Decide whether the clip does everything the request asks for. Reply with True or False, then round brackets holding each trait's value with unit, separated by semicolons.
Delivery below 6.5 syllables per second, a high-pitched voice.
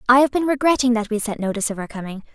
False (7.7 syllables/s; 235 Hz)